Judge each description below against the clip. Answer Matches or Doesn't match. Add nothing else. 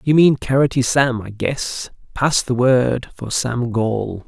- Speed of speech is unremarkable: Matches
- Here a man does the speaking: Matches